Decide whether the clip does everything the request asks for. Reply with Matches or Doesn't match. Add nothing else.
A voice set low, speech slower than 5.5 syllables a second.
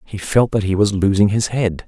Matches